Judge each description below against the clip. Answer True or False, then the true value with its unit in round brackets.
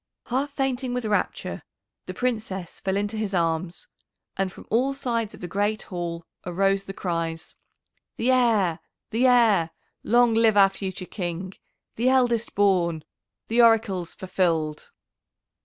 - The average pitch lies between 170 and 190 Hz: False (200 Hz)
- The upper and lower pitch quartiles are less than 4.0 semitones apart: False (4.8 semitones)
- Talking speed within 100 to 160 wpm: True (140 wpm)